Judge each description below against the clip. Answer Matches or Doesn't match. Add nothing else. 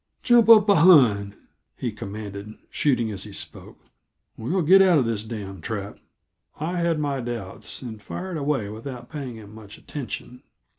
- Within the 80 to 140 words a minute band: Doesn't match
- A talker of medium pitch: Doesn't match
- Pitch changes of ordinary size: Doesn't match